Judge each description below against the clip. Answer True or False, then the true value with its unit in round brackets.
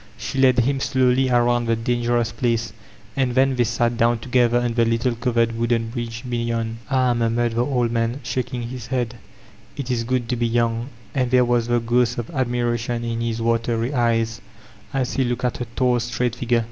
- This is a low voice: True (120 Hz)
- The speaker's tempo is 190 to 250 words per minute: True (200 wpm)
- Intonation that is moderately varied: False (1.2 semitones)